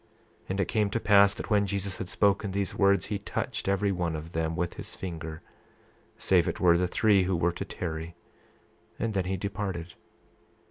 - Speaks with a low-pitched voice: Yes, very low, 95 Hz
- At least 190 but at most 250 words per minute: Yes, average, 195 wpm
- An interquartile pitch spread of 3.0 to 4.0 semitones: No, narrow, 2.6 semitones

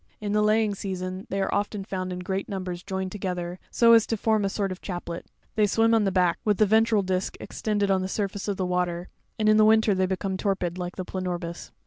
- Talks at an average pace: No, fast, 240 wpm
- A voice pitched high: Yes, high, 195 Hz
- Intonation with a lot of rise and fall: No, narrow, 2.4 semitones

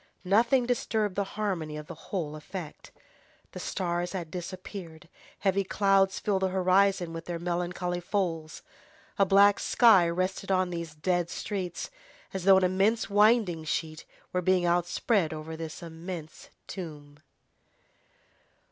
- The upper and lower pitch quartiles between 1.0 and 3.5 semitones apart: Yes, average, 2.8 semitones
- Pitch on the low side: No, medium, 180 Hz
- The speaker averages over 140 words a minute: No, slow, 135 wpm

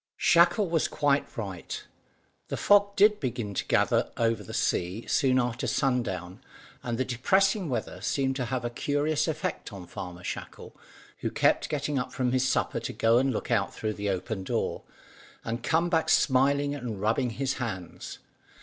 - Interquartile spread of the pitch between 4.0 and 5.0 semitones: Yes, average, 4.3 semitones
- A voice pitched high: No, low, 125 Hz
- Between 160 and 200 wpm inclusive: Yes, average, 170 wpm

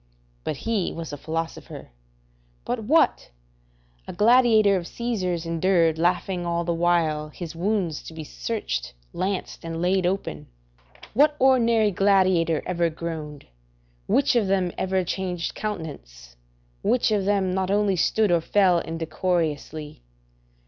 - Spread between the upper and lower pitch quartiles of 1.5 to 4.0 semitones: Yes, average, 3.6 semitones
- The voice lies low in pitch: No, medium, 180 Hz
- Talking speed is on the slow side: Yes, slow, 130 wpm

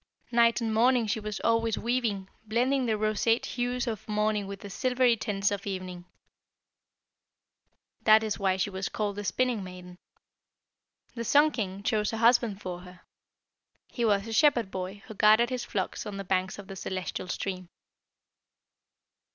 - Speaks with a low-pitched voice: No, high, 215 Hz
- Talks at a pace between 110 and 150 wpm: No, average, 160 wpm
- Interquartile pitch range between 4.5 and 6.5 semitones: No, average, 3.2 semitones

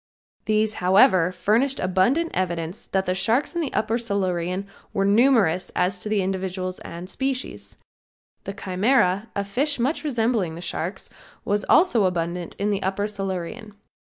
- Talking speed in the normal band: Yes, average, 145 wpm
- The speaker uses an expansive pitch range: No, average, 3.7 semitones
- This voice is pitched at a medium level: No, high, 195 Hz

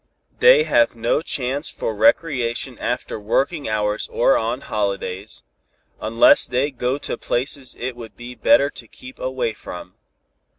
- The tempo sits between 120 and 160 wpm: Yes, average, 140 wpm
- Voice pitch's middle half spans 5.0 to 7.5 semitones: No, average, 3.5 semitones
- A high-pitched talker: No, low, 120 Hz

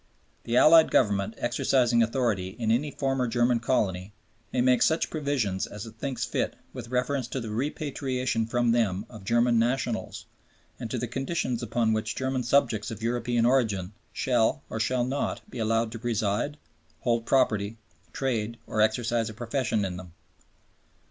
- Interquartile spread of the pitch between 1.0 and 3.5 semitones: Yes, narrow, 2.6 semitones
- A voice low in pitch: Yes, low, 120 Hz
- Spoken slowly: No, average, 160 wpm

